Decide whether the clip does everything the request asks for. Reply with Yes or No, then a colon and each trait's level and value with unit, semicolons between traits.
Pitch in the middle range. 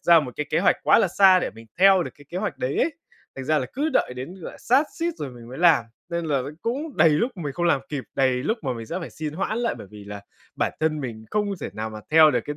Yes: medium, 155 Hz